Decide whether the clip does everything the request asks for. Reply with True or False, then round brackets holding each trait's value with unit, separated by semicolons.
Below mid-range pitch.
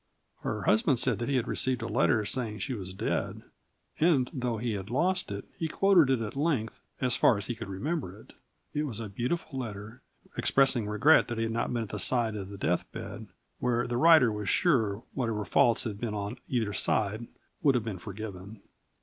True (115 Hz)